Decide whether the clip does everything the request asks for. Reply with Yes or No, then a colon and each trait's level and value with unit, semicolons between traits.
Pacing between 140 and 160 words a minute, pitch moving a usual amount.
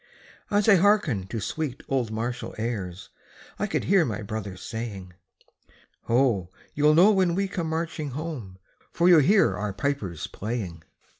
No: average, 150 wpm; wide, 8.2 semitones